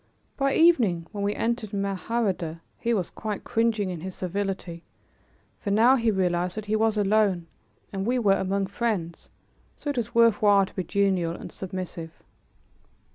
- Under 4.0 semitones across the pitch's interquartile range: Yes, average, 3.4 semitones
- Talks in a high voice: Yes, high, 200 Hz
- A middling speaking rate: Yes, average, 165 wpm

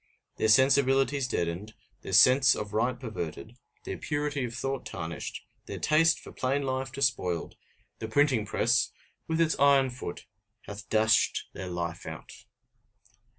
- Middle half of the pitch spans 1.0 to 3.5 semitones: No, average, 4.6 semitones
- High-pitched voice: No, low, 125 Hz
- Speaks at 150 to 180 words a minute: No, average, 140 wpm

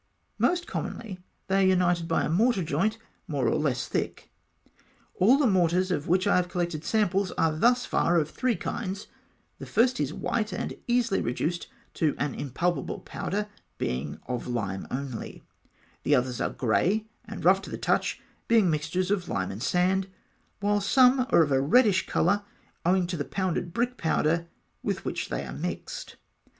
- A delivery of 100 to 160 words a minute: No, average, 170 wpm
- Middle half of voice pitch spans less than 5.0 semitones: No, average, 5.3 semitones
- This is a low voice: No, medium, 180 Hz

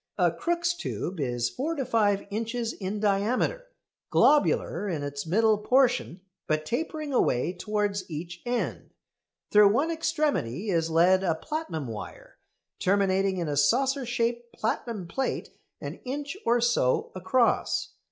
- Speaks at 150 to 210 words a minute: No, slow, 135 wpm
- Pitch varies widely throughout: Yes, wide, 6.6 semitones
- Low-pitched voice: No, high, 210 Hz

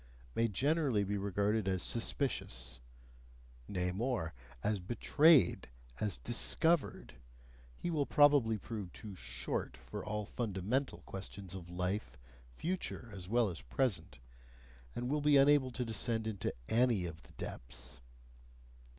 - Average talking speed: No, slow, 125 wpm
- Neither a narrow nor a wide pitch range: No, wide, 5.9 semitones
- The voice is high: No, low, 105 Hz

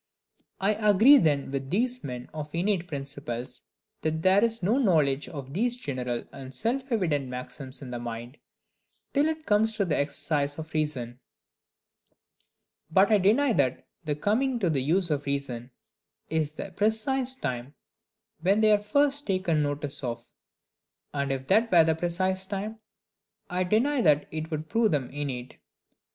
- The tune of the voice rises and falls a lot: Yes, wide, 7.2 semitones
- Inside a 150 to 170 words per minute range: Yes, average, 160 wpm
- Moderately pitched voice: Yes, medium, 160 Hz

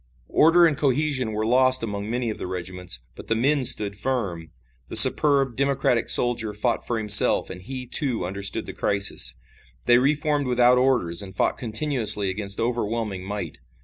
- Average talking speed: Yes, average, 170 wpm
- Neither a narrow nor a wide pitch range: Yes, average, 4.6 semitones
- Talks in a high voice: No, low, 115 Hz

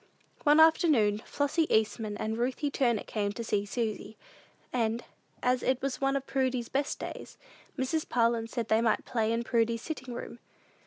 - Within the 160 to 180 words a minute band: Yes, average, 165 wpm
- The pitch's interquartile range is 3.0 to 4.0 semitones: Yes, average, 3.4 semitones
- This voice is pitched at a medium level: No, high, 235 Hz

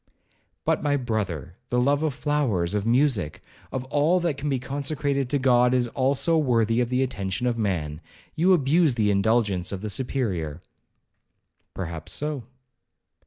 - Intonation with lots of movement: Yes, wide, 5.8 semitones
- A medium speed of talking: Yes, average, 150 wpm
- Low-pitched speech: Yes, low, 125 Hz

